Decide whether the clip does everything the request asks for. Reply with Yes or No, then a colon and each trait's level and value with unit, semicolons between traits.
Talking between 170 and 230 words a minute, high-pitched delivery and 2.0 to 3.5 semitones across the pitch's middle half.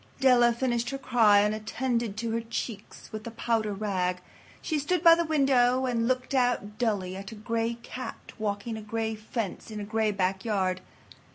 Yes: average, 180 wpm; high, 225 Hz; average, 2.9 semitones